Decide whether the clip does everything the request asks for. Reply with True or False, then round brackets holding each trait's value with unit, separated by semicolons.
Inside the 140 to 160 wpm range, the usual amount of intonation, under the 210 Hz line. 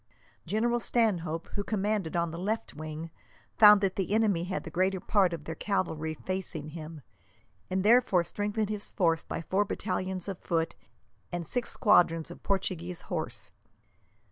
True (155 wpm; 3.8 semitones; 185 Hz)